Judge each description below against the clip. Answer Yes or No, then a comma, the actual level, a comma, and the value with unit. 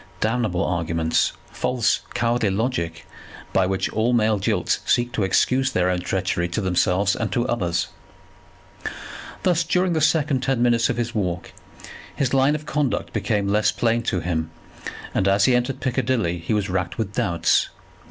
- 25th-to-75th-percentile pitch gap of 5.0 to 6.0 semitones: Yes, wide, 5.4 semitones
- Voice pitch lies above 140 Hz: No, low, 110 Hz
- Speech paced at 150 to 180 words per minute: Yes, average, 160 wpm